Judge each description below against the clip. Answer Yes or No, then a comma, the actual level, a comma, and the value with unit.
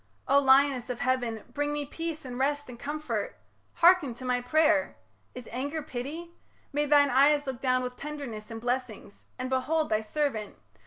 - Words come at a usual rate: Yes, average, 170 wpm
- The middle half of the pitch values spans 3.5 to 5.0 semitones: No, average, 3.0 semitones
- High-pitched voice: Yes, very high, 270 Hz